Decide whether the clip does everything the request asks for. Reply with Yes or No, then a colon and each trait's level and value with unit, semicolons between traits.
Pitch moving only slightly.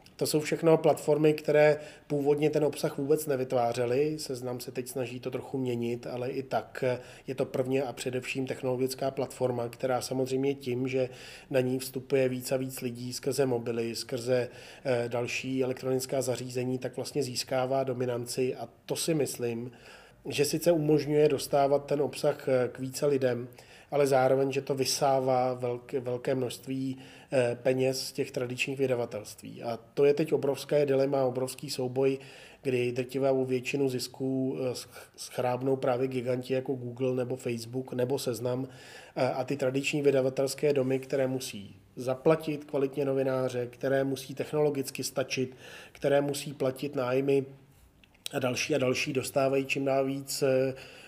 Yes: narrow, 1.6 semitones